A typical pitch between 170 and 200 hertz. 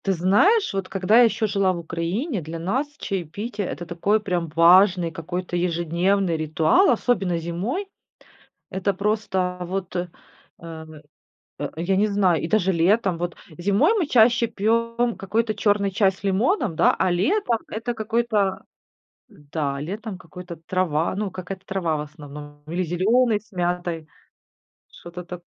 Yes: high, 190 Hz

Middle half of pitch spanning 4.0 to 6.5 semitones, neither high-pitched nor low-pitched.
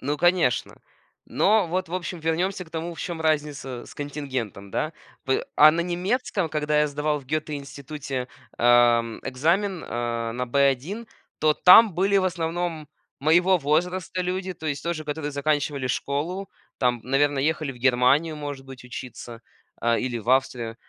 Yes: average, 4.7 semitones; medium, 150 Hz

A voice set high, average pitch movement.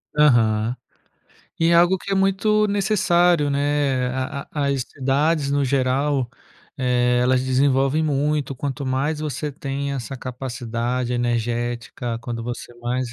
No: low, 135 Hz; average, 3.3 semitones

